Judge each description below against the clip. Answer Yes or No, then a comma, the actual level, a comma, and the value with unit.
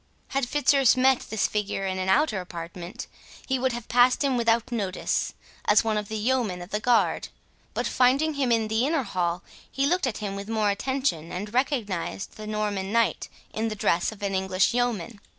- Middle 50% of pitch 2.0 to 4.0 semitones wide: No, average, 4.4 semitones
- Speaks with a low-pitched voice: No, high, 220 Hz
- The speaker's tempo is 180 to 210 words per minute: Yes, average, 195 wpm